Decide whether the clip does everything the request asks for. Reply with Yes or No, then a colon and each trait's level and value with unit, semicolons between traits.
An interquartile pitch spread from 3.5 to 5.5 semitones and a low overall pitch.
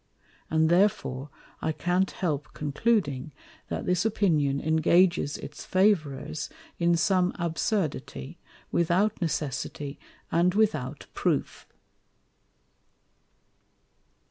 No: average, 4.1 semitones; medium, 170 Hz